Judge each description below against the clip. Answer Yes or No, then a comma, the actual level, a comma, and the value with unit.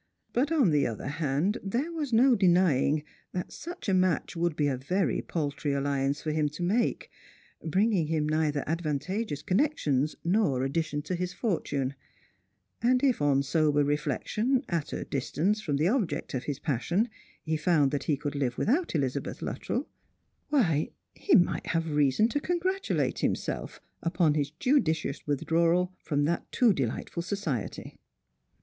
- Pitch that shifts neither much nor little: No, wide, 5.9 semitones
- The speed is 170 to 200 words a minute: No, average, 155 wpm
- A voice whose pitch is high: No, medium, 160 Hz